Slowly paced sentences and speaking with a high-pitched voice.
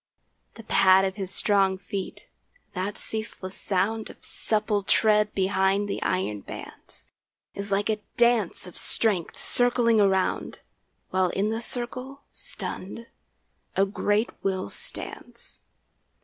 Yes: slow, 120 wpm; high, 200 Hz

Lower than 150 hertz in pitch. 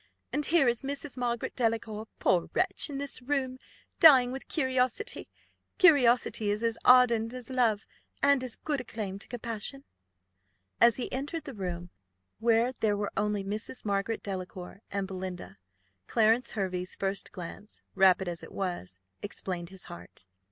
No: high, 225 Hz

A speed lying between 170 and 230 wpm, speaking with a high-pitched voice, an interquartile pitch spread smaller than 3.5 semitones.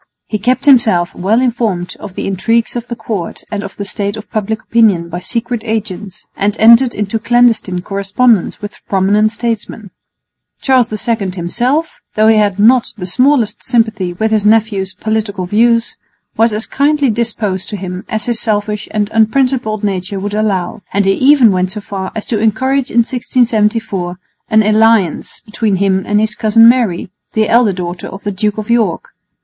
Yes: average, 175 wpm; high, 215 Hz; average, 2.9 semitones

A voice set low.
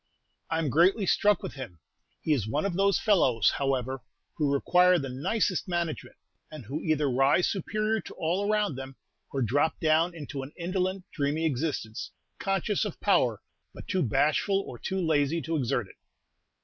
No: medium, 160 Hz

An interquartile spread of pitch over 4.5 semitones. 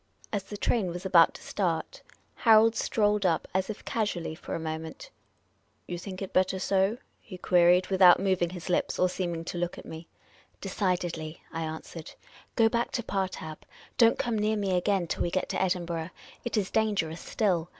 No: average, 3.2 semitones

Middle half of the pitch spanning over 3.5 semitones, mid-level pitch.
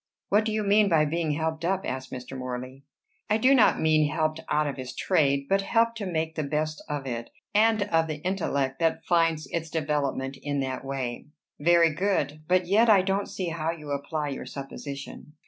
Yes: average, 4.7 semitones; medium, 155 Hz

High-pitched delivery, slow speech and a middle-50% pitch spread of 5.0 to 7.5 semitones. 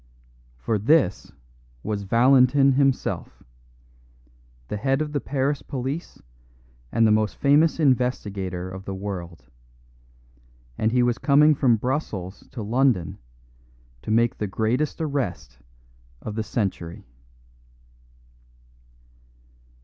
No: low, 120 Hz; slow, 105 wpm; wide, 5.4 semitones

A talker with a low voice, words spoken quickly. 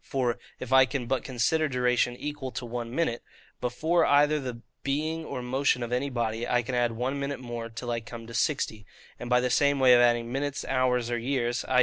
Yes: low, 125 Hz; fast, 220 wpm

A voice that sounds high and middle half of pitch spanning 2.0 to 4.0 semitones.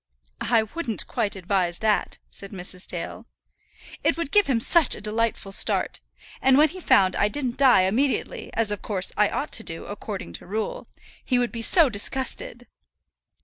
No: high, 225 Hz; average, 4.8 semitones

